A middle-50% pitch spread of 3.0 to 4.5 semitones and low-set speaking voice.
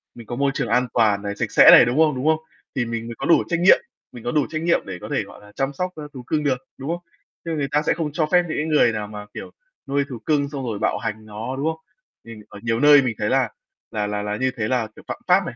No: average, 5.2 semitones; low, 130 Hz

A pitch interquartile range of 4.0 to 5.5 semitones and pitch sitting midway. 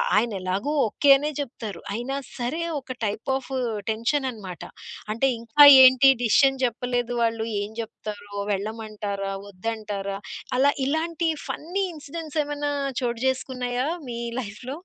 No: average, 4.3 semitones; high, 240 Hz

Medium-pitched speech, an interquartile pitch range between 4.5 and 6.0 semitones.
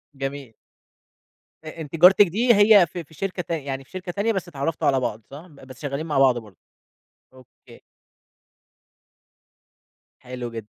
Yes: medium, 150 Hz; average, 5.2 semitones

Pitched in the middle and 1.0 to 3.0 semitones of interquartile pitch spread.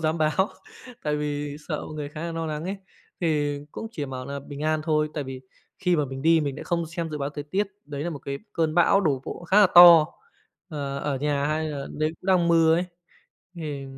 Yes: medium, 155 Hz; narrow, 2.4 semitones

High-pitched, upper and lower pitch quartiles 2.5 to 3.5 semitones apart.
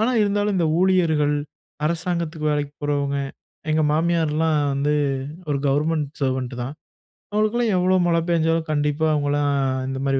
No: medium, 155 Hz; average, 2.8 semitones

